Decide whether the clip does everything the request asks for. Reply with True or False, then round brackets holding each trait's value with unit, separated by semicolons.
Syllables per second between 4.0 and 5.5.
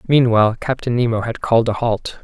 False (5.9 syllables/s)